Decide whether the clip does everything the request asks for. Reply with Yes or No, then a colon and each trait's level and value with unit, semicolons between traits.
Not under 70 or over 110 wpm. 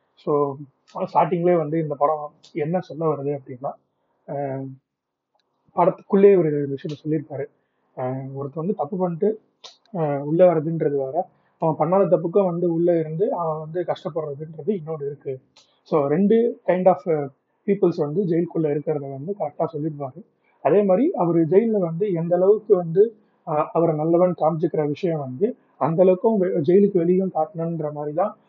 No: fast, 130 wpm